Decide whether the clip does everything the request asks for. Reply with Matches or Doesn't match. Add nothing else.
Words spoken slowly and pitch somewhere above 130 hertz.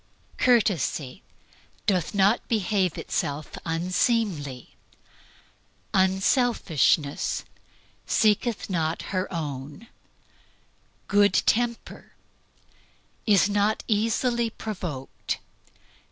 Matches